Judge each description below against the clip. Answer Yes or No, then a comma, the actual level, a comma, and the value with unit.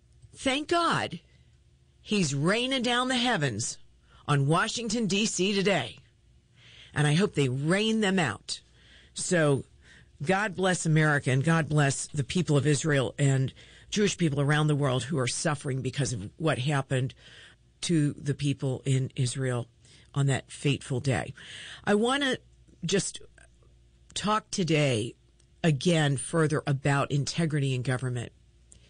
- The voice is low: No, medium, 145 Hz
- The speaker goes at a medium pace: No, slow, 130 wpm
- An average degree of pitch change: No, wide, 5.7 semitones